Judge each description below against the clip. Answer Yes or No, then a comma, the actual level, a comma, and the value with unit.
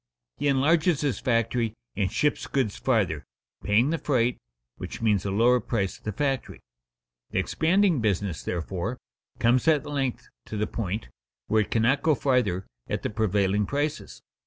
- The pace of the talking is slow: No, average, 160 wpm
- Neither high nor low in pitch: No, low, 115 Hz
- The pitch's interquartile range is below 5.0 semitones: No, average, 5.3 semitones